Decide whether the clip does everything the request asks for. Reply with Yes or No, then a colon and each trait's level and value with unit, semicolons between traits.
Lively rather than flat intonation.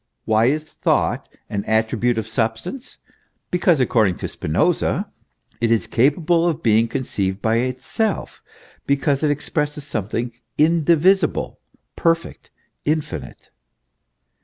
Yes: wide, 6.0 semitones